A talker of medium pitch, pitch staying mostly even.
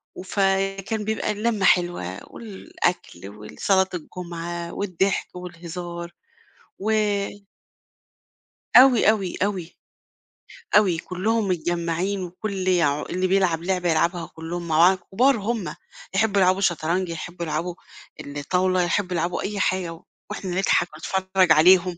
Yes: medium, 180 Hz; narrow, 2.3 semitones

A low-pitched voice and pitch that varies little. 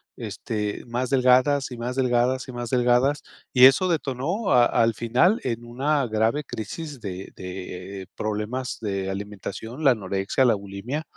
No: low, 120 Hz; average, 3.9 semitones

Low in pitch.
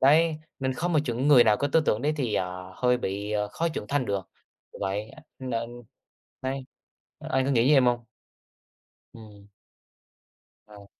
Yes: low, 120 Hz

